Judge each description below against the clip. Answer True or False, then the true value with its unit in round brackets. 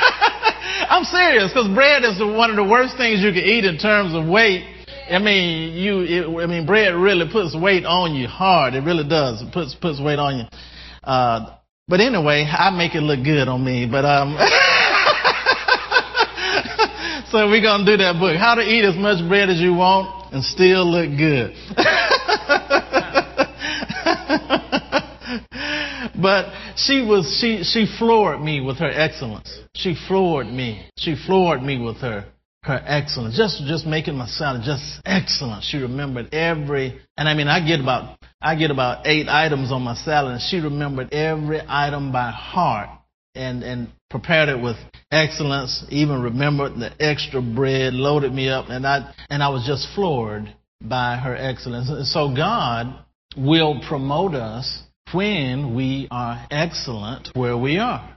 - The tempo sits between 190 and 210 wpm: False (165 wpm)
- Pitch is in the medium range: True (155 Hz)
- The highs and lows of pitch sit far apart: True (6.7 semitones)